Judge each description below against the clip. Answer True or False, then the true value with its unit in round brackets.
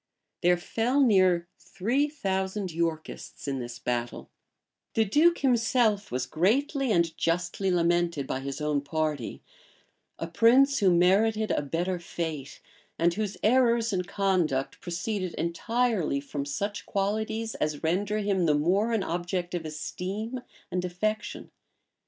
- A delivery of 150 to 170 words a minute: False (135 wpm)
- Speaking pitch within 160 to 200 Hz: True (185 Hz)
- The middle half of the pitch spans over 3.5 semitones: True (4.7 semitones)